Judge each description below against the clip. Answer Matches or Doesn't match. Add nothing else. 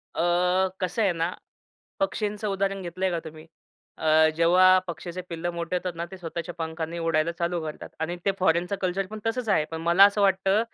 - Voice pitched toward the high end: Doesn't match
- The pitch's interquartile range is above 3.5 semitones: Doesn't match